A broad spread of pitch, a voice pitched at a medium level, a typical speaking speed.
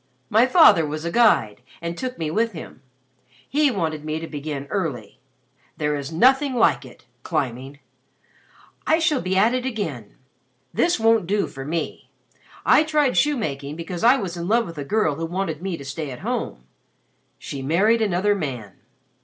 Yes: wide, 7.5 semitones; medium, 170 Hz; average, 170 wpm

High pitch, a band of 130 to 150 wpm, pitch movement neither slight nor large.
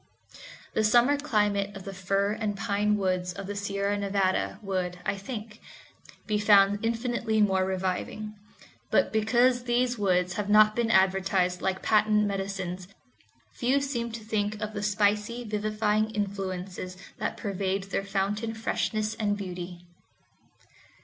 No: high, 205 Hz; slow, 135 wpm; narrow, 2.0 semitones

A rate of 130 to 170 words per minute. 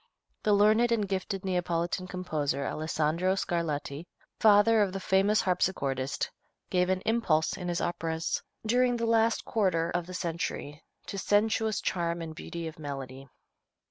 Yes: average, 140 wpm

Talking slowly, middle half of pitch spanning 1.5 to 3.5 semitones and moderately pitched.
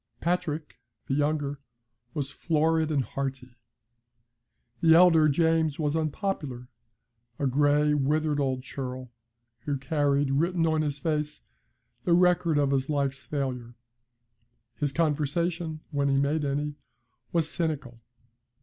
Yes: slow, 120 wpm; narrow, 2.5 semitones; medium, 150 Hz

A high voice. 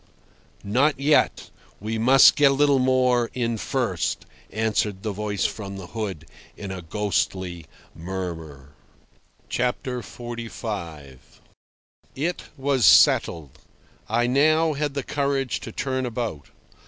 No: low, 115 Hz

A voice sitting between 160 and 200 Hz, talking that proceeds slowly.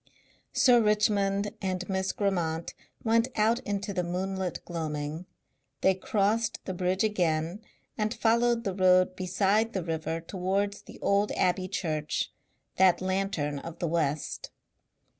Yes: high, 190 Hz; slow, 130 wpm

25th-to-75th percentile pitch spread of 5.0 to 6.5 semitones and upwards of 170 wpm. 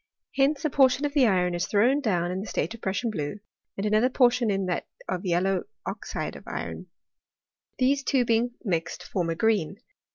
Yes: wide, 5.6 semitones; average, 195 wpm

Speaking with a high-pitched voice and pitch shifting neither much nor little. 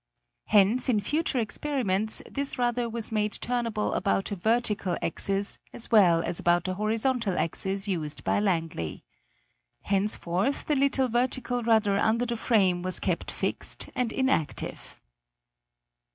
Yes: high, 215 Hz; average, 4.1 semitones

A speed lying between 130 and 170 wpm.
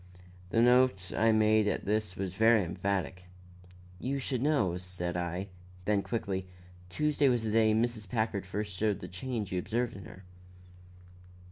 Yes: average, 155 wpm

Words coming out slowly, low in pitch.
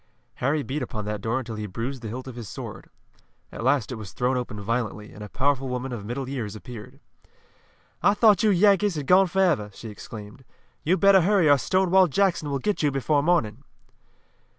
No: average, 195 wpm; low, 130 Hz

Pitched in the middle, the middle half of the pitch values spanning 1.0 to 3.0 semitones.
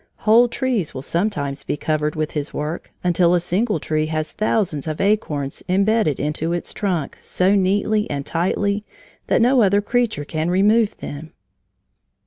No: medium, 180 Hz; average, 5.3 semitones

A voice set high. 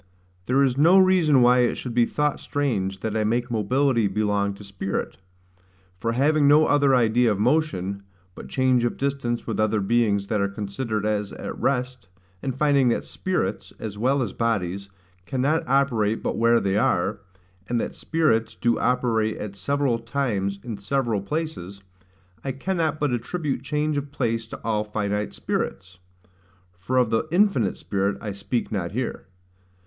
No: low, 120 Hz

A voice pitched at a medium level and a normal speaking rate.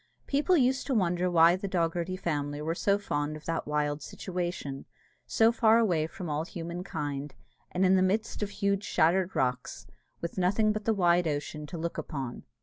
Yes: medium, 175 Hz; average, 185 wpm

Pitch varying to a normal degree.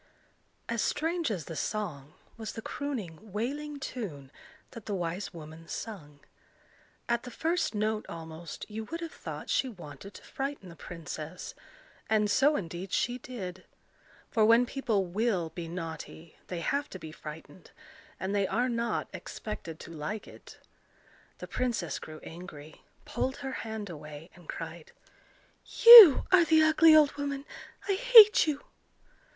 No: wide, 8.2 semitones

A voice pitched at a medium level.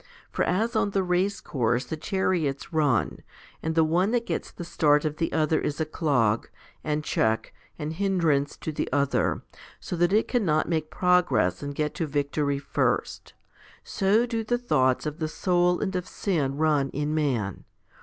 Yes: medium, 155 Hz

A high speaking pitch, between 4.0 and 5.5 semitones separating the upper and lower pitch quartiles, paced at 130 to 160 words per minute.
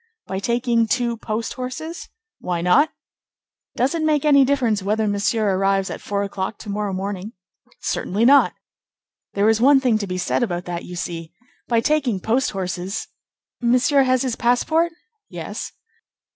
Yes: high, 225 Hz; average, 4.8 semitones; average, 155 wpm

